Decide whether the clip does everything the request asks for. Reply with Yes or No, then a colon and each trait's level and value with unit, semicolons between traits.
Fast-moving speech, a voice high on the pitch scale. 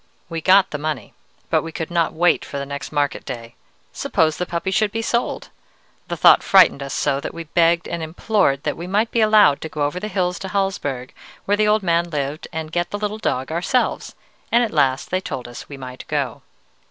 No: fast, 220 wpm; medium, 170 Hz